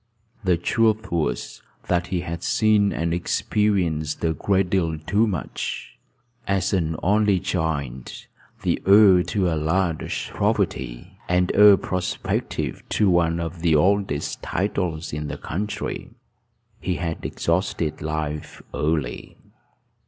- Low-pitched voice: Yes, very low, 85 Hz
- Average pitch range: Yes, average, 3.6 semitones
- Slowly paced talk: Yes, slow, 125 wpm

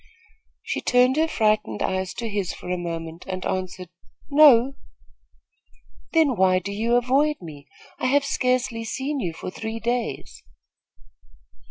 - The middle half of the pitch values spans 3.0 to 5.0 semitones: No, wide, 5.6 semitones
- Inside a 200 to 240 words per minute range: No, average, 140 wpm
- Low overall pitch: No, high, 225 Hz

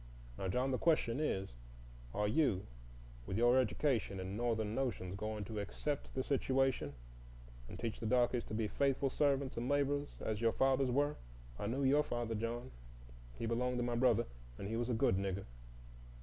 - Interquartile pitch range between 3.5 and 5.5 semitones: Yes, average, 4.2 semitones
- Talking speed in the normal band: Yes, average, 175 wpm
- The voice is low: Yes, low, 120 Hz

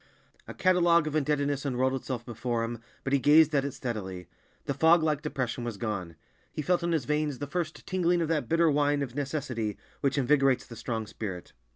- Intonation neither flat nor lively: Yes, average, 4.4 semitones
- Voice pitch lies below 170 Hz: Yes, medium, 140 Hz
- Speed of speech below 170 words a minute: No, average, 200 wpm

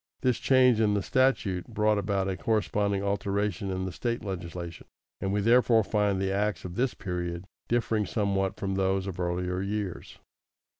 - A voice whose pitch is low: Yes, low, 100 Hz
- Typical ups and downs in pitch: No, narrow, 2.3 semitones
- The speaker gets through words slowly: No, average, 165 wpm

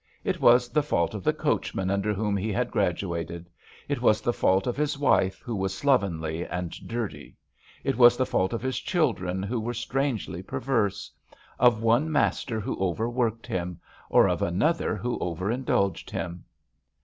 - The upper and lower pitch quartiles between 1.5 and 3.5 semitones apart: No, average, 4.8 semitones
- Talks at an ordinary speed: Yes, average, 170 wpm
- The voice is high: No, low, 110 Hz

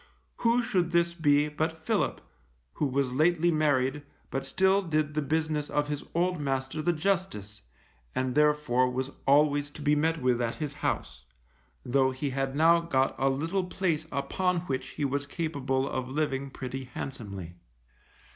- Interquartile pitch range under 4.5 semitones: Yes, average, 3.4 semitones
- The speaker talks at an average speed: Yes, average, 160 wpm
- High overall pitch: No, medium, 145 Hz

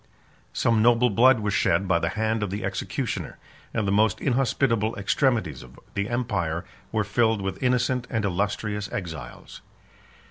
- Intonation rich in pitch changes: No, average, 3.3 semitones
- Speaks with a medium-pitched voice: No, low, 105 Hz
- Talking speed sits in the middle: Yes, average, 150 wpm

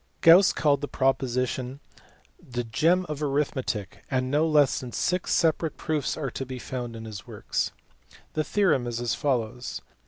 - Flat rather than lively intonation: No, average, 3.9 semitones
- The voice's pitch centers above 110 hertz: Yes, low, 135 Hz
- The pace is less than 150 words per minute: No, average, 165 wpm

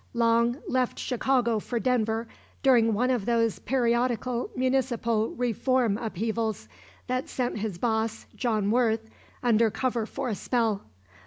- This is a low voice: No, high, 235 Hz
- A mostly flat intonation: Yes, narrow, 2.1 semitones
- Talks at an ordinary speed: No, slow, 130 wpm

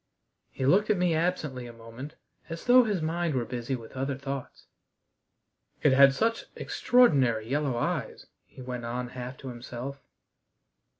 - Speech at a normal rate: Yes, average, 155 wpm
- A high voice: No, low, 135 Hz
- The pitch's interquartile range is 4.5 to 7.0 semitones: Yes, average, 4.9 semitones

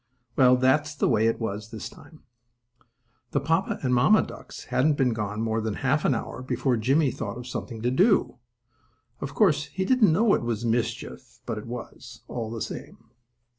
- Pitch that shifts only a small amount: No, average, 4.6 semitones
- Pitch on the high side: No, low, 125 Hz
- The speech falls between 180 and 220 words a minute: Yes, average, 185 wpm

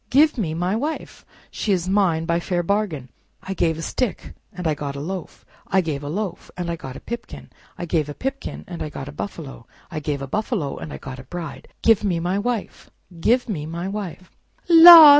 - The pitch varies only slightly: No, average, 5.1 semitones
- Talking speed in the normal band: No, fast, 220 wpm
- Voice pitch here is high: No, medium, 175 Hz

